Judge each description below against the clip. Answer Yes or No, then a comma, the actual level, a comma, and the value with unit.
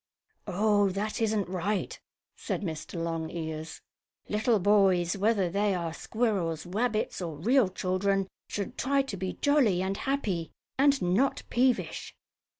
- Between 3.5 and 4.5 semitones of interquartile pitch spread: Yes, average, 3.8 semitones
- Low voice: No, high, 195 Hz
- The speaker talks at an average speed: No, slow, 130 wpm